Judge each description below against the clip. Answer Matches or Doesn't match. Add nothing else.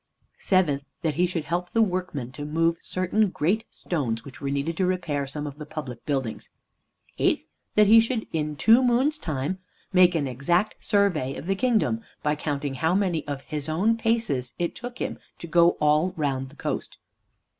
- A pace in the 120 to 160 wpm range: Doesn't match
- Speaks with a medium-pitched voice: Matches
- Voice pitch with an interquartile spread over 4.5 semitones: Matches